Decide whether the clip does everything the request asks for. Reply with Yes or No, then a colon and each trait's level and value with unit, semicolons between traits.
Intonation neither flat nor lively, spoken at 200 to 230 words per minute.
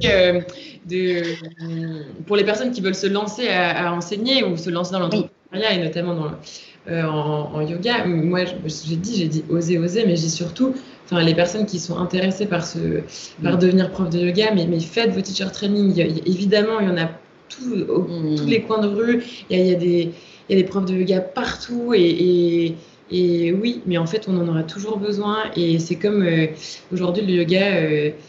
Yes: average, 3.4 semitones; average, 215 wpm